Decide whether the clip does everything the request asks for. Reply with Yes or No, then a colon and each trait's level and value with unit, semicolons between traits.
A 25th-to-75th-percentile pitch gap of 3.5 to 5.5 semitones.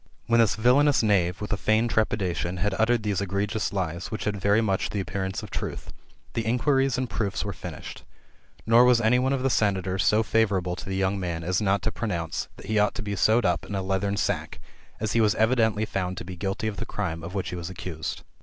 No: average, 2.9 semitones